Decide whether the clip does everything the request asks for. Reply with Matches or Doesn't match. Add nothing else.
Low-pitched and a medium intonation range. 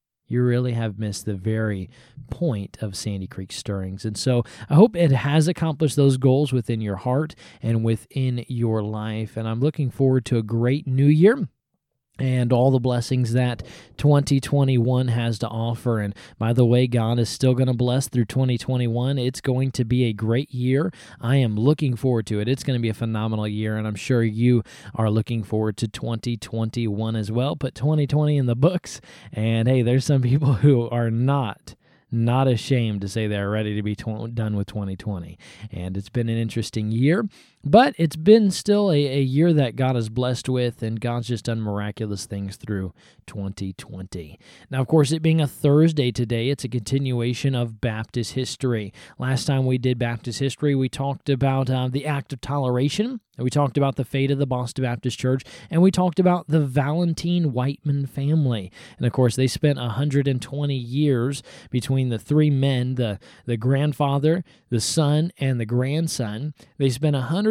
Matches